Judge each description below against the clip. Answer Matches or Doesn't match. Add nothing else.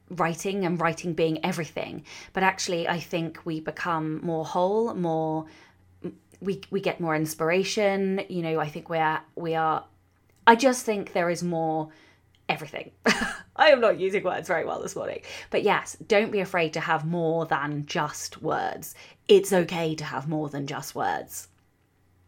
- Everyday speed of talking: Matches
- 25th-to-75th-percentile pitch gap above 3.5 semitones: Doesn't match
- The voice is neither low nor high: Matches